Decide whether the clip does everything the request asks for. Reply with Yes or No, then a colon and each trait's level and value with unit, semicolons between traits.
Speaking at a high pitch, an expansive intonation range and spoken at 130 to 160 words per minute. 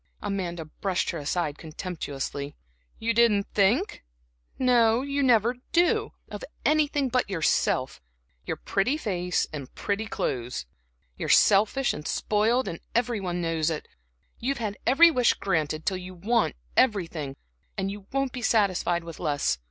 Yes: high, 200 Hz; wide, 6.4 semitones; average, 140 wpm